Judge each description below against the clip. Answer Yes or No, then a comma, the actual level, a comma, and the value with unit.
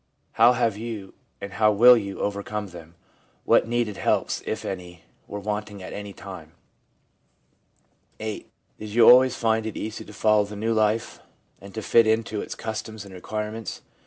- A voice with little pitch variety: Yes, narrow, 1.9 semitones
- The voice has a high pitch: No, low, 105 Hz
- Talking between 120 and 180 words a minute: Yes, average, 170 wpm